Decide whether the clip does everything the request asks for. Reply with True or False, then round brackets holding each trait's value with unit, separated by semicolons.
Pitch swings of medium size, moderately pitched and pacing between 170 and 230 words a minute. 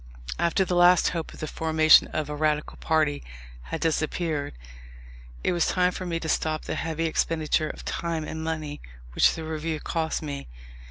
False (1.3 semitones; 160 Hz; 175 wpm)